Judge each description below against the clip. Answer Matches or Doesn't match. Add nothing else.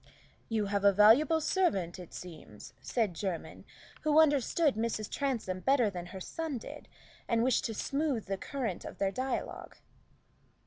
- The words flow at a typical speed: Matches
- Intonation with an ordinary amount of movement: Doesn't match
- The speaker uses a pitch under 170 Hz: Doesn't match